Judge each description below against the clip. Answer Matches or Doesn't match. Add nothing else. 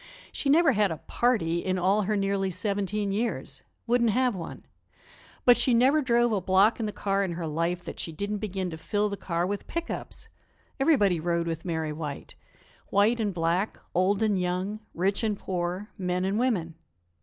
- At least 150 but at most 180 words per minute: Doesn't match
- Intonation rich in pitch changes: Doesn't match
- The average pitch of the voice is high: Matches